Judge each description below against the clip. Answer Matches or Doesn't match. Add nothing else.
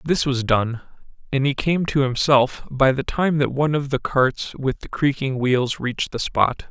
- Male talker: Matches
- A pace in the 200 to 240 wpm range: Matches